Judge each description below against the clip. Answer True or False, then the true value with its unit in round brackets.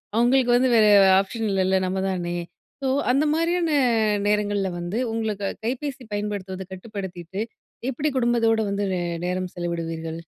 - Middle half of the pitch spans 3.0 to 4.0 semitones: False (4.4 semitones)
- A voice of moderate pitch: False (205 Hz)